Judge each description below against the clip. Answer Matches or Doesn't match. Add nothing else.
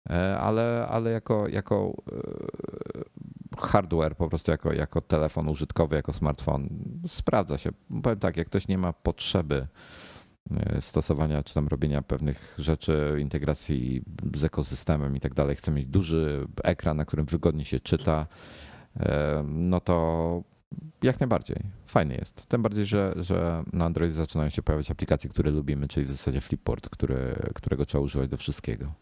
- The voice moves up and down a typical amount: Matches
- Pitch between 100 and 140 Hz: Doesn't match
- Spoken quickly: Doesn't match